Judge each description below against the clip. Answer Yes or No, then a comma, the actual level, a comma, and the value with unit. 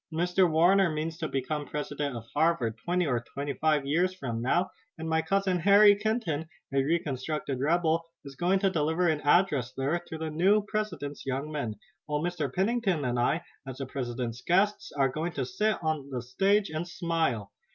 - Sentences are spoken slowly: No, average, 185 wpm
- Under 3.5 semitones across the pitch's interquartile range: No, average, 4.4 semitones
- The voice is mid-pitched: Yes, medium, 160 Hz